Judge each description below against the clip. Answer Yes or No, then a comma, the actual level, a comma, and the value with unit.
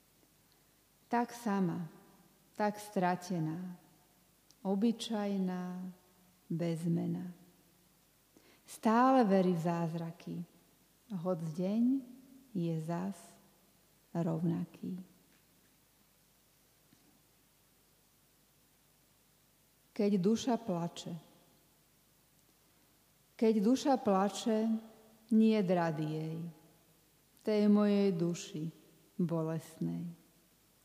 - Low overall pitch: No, medium, 180 Hz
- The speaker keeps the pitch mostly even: No, average, 3.7 semitones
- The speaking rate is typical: No, slow, 55 wpm